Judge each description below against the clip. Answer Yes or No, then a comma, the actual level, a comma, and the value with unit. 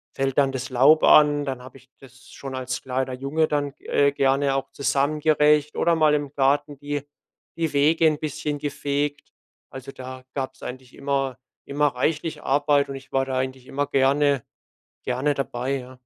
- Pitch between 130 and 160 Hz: Yes, medium, 140 Hz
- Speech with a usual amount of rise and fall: No, narrow, 1.8 semitones